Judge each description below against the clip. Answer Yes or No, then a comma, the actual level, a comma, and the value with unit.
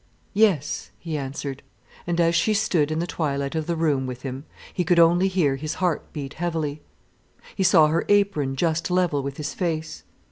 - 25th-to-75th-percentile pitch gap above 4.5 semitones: No, average, 3.5 semitones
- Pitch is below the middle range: No, medium, 160 Hz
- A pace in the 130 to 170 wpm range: No, average, 185 wpm